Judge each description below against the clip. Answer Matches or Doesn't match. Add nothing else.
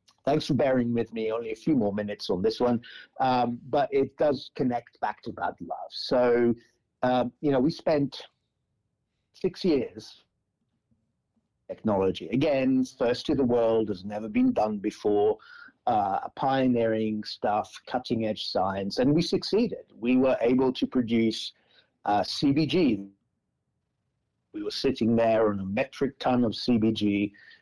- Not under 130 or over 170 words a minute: Matches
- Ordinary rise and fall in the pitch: Matches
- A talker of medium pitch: Doesn't match